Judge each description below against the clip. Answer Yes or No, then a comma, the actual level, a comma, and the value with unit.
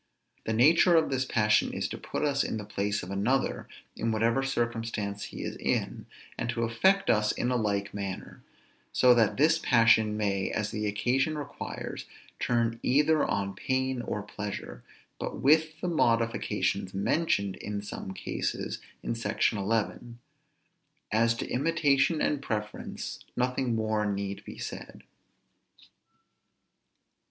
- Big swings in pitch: No, average, 4.3 semitones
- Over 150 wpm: No, average, 140 wpm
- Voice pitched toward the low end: Yes, low, 115 Hz